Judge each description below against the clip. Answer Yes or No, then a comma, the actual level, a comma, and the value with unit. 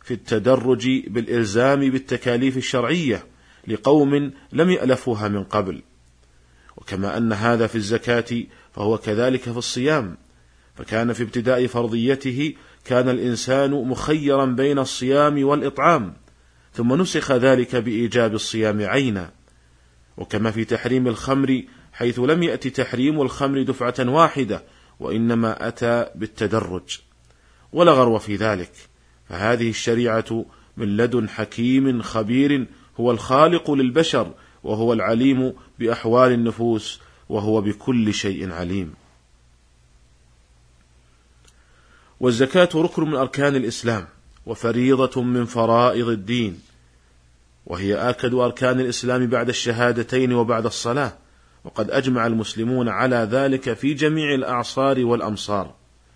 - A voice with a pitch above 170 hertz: No, low, 120 Hz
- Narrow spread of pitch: No, average, 4.4 semitones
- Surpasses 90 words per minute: Yes, average, 105 wpm